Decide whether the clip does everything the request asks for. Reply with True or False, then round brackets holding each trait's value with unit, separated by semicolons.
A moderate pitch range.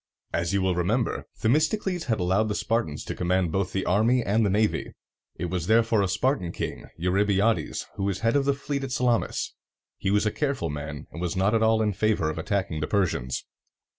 True (4.1 semitones)